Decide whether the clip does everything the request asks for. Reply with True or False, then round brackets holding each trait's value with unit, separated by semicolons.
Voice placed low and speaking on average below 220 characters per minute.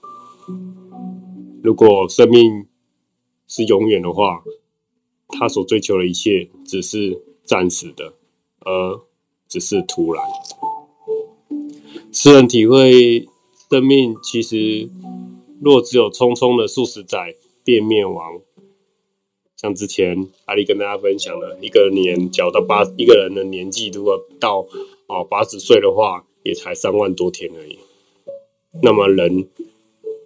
True (125 Hz; 175 characters per minute)